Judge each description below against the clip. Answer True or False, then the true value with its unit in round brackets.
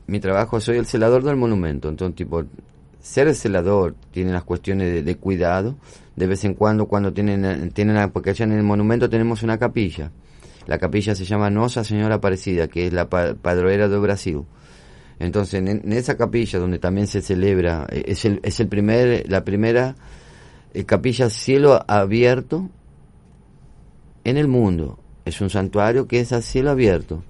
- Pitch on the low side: True (100 Hz)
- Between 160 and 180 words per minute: True (170 wpm)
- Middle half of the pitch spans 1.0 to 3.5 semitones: False (4.1 semitones)